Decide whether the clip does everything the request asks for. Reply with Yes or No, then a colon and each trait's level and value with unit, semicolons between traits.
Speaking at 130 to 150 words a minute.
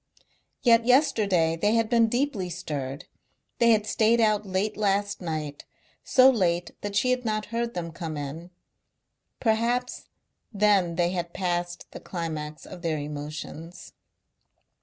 Yes: average, 140 wpm